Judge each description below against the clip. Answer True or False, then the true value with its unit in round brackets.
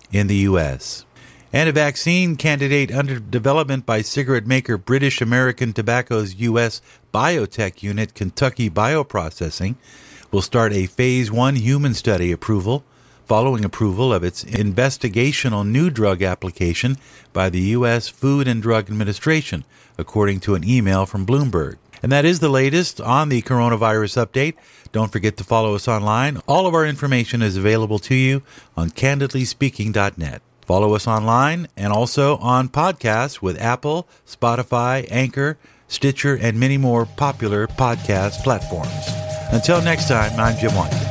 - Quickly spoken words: False (145 wpm)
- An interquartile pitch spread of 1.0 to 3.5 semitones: False (4.3 semitones)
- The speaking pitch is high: False (120 Hz)